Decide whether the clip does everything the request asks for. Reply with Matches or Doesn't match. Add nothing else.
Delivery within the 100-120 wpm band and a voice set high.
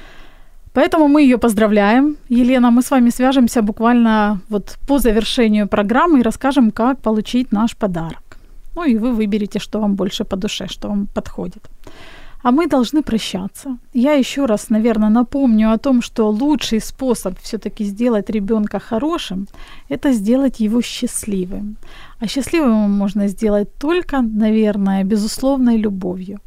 Doesn't match